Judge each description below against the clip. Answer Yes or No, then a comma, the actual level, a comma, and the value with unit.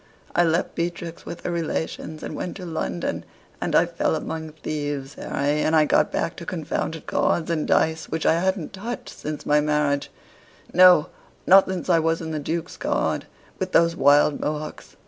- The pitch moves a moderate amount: No, narrow, 2.3 semitones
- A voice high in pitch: No, medium, 160 Hz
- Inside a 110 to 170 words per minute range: No, average, 180 wpm